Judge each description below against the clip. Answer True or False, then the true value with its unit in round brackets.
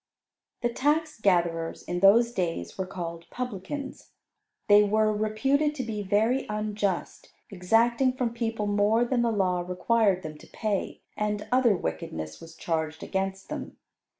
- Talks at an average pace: True (145 wpm)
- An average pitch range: True (4.6 semitones)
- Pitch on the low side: False (210 Hz)